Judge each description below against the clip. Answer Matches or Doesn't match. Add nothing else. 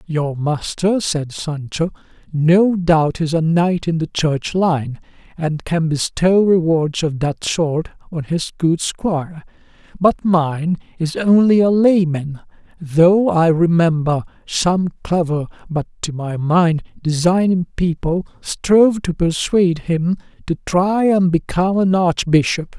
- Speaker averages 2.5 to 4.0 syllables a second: Matches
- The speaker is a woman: Doesn't match